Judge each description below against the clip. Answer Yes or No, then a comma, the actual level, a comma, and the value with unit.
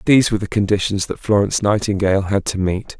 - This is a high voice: No, low, 100 Hz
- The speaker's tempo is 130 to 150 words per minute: No, average, 200 wpm